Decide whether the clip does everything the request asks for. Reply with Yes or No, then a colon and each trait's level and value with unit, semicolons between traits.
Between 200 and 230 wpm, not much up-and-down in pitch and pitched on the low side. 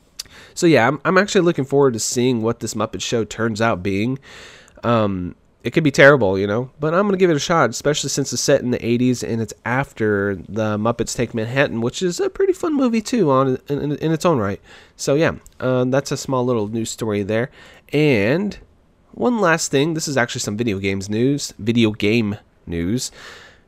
No: fast, 205 wpm; average, 4.7 semitones; low, 125 Hz